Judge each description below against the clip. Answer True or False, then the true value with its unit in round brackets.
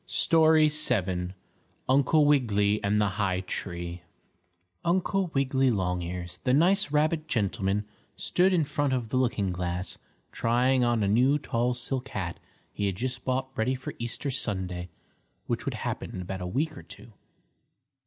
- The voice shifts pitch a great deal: True (6.6 semitones)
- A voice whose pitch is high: False (120 Hz)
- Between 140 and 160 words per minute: True (155 wpm)